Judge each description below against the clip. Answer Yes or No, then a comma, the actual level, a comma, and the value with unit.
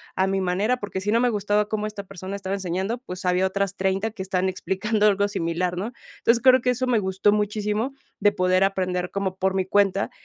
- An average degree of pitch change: No, narrow, 2.0 semitones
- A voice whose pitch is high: Yes, high, 195 Hz